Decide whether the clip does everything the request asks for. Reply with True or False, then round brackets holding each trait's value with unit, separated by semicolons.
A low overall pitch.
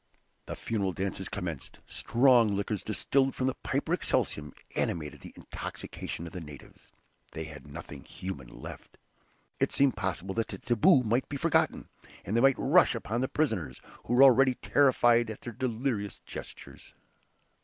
True (115 Hz)